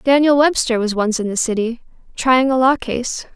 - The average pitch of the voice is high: Yes, very high, 250 Hz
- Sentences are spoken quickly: No, average, 195 wpm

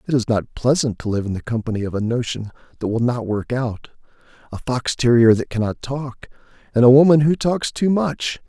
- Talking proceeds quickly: Yes, fast, 210 wpm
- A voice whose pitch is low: Yes, low, 125 Hz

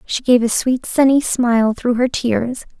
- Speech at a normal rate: Yes, average, 195 wpm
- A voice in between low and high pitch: No, high, 245 Hz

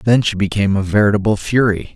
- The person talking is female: No, male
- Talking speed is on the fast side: No, average, 185 wpm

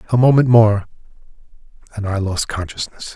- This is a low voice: Yes, low, 110 Hz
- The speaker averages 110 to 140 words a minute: Yes, slow, 135 wpm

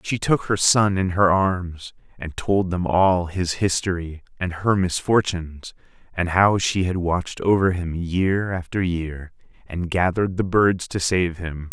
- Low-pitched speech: Yes, very low, 90 Hz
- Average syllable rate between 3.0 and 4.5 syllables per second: Yes, 4.1 syllables/s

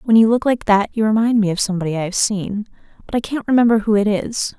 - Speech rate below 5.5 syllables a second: No, 6.4 syllables/s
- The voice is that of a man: No, female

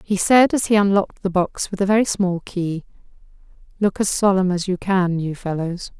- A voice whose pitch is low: No, high, 190 Hz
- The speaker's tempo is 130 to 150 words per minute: No, average, 200 wpm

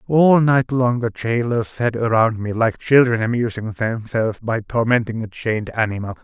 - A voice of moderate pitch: No, low, 115 Hz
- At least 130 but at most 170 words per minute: Yes, average, 165 wpm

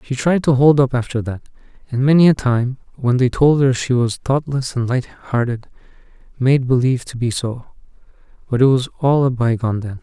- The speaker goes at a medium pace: Yes, average, 190 wpm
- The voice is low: Yes, low, 130 Hz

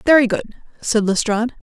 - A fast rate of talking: No, average, 140 wpm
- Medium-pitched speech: No, high, 230 Hz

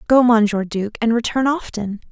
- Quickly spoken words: No, average, 170 wpm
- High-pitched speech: Yes, high, 230 Hz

